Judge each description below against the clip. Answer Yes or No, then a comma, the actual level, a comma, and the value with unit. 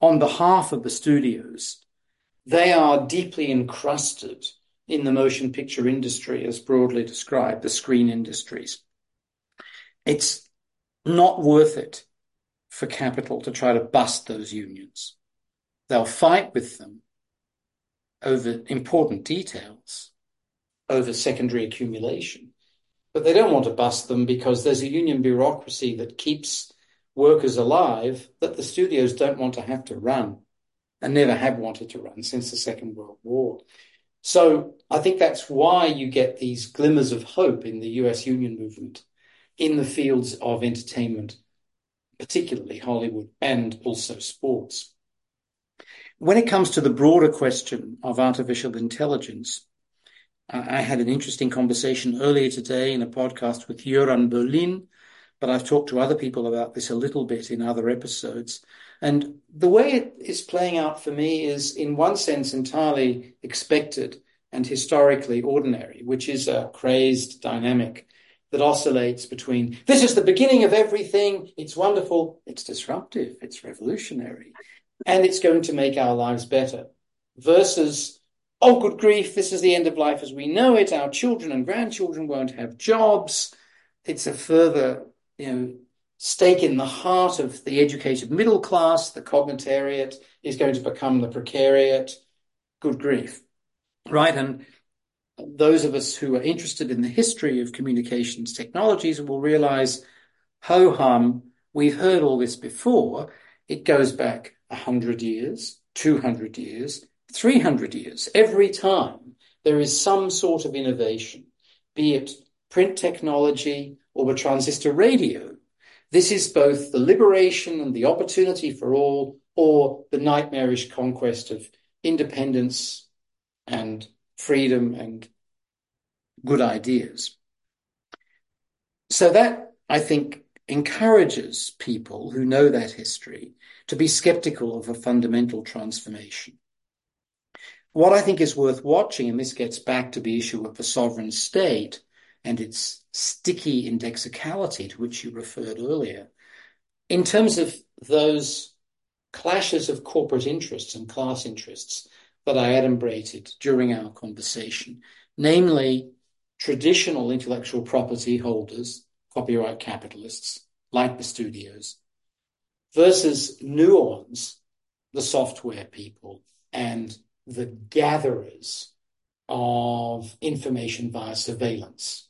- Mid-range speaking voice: No, low, 130 Hz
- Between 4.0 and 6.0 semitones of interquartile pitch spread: Yes, average, 4.4 semitones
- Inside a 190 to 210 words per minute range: No, slow, 135 wpm